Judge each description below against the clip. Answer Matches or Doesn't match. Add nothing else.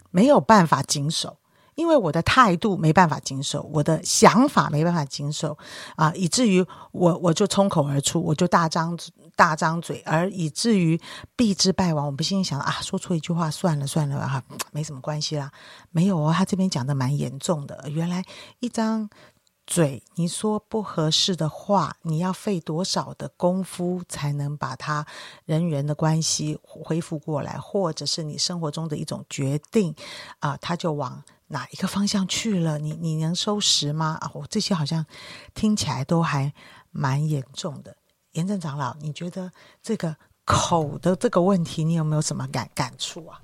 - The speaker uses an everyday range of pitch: Matches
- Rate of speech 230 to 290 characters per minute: Matches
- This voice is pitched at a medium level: Matches